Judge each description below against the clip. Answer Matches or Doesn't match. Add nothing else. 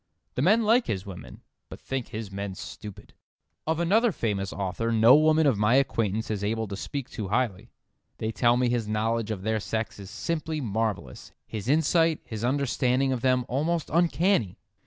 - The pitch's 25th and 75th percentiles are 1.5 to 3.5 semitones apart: Doesn't match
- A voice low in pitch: Matches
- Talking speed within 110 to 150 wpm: Doesn't match